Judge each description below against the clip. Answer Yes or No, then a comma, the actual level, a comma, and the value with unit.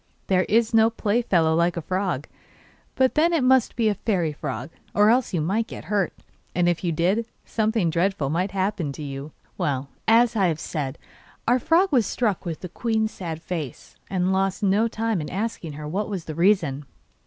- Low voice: No, high, 190 Hz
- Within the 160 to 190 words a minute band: No, average, 200 wpm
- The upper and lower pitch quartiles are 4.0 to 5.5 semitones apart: Yes, average, 5.2 semitones